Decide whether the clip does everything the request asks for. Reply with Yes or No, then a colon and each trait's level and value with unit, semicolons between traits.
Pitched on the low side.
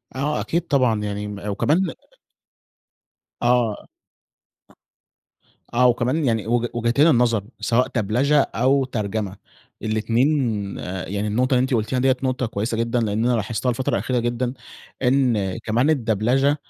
Yes: low, 120 Hz